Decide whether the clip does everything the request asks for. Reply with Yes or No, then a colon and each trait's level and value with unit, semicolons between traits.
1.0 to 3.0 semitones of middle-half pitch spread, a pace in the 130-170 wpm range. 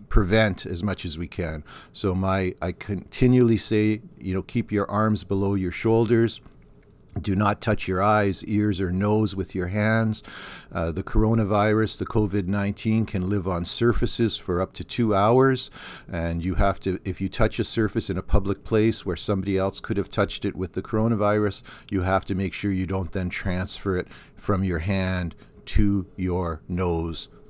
No: narrow, 2.6 semitones; average, 185 wpm